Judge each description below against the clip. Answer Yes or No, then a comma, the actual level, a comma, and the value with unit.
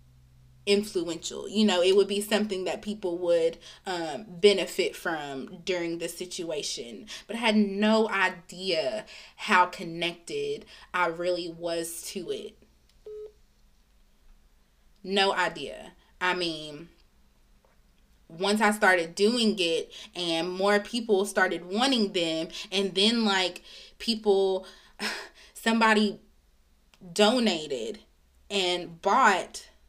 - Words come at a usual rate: No, slow, 100 wpm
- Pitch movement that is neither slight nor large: Yes, average, 3.5 semitones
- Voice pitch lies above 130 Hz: Yes, high, 190 Hz